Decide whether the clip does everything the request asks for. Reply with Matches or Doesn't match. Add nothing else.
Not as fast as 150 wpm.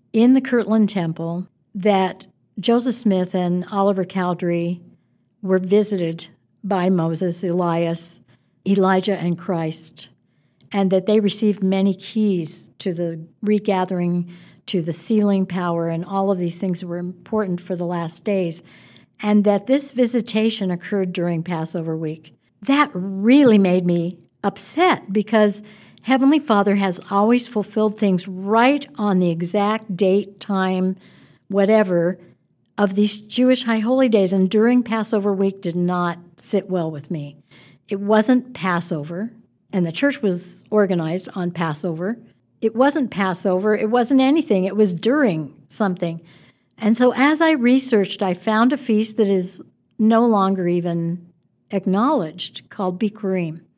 Matches